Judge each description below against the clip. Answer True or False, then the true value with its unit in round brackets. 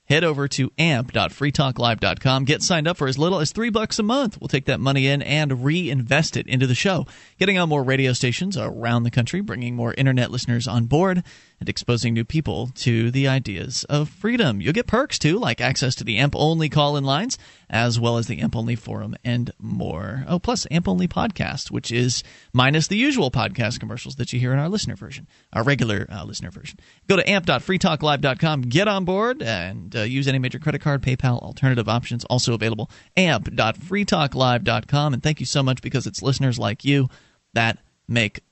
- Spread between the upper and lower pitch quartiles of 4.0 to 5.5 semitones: True (4.7 semitones)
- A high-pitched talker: False (135 Hz)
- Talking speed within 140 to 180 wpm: False (195 wpm)